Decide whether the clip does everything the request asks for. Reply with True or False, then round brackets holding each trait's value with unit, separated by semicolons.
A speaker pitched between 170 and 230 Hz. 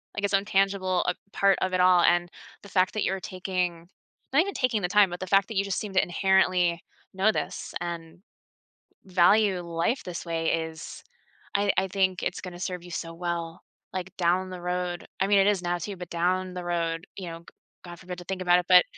True (185 Hz)